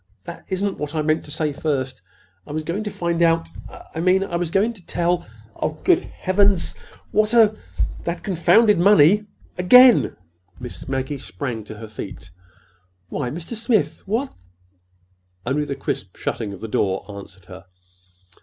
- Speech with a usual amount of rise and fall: No, wide, 7.0 semitones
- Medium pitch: Yes, medium, 165 Hz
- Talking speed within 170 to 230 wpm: No, average, 150 wpm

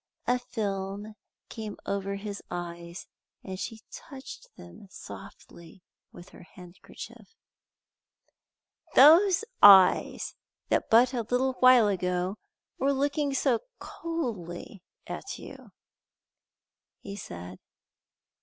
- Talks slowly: Yes, slow, 100 wpm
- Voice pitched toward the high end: Yes, high, 205 Hz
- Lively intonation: Yes, wide, 5.8 semitones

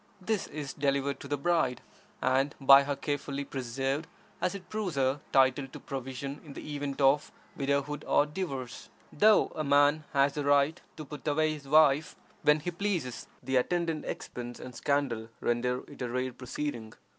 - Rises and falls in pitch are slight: Yes, narrow, 2.2 semitones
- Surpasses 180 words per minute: No, average, 170 wpm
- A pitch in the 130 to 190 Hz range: Yes, medium, 140 Hz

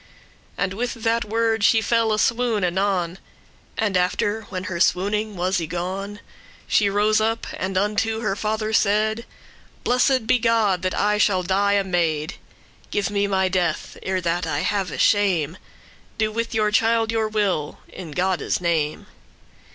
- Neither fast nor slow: Yes, average, 160 wpm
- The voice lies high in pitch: Yes, high, 205 Hz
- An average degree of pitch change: Yes, average, 3.0 semitones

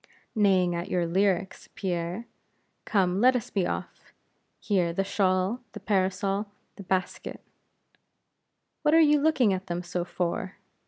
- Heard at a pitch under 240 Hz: Yes, high, 190 Hz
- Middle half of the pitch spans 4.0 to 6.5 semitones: No, narrow, 2.6 semitones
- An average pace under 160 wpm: Yes, average, 140 wpm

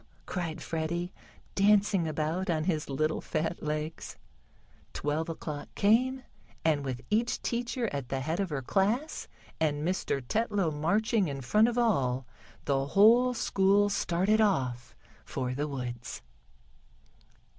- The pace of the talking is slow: Yes, slow, 130 wpm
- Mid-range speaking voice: Yes, medium, 165 Hz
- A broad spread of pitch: Yes, wide, 6.2 semitones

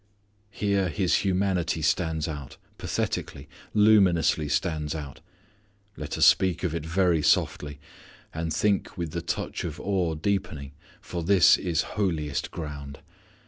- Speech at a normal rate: No, slow, 130 wpm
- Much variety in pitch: No, average, 3.7 semitones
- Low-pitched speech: Yes, very low, 85 Hz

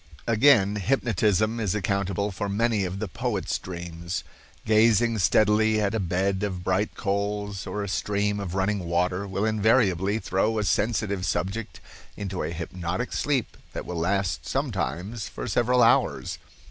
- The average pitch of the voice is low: Yes, low, 100 Hz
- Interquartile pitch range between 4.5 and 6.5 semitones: No, narrow, 2.6 semitones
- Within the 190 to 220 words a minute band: No, average, 145 wpm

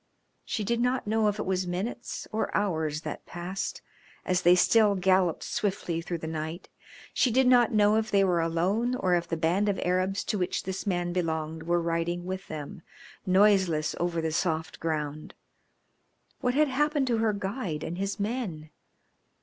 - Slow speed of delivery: No, average, 175 wpm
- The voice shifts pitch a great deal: No, average, 4.1 semitones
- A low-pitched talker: No, medium, 185 Hz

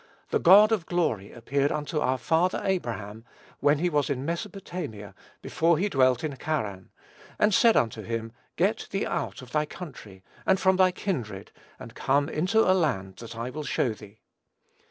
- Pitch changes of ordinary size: No, wide, 7.5 semitones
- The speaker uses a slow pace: No, average, 175 wpm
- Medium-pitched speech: Yes, medium, 145 Hz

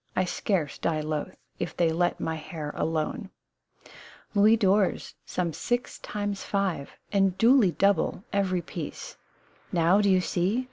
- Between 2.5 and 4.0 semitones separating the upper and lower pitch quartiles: Yes, average, 3.7 semitones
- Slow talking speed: No, average, 145 wpm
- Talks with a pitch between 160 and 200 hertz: Yes, medium, 185 Hz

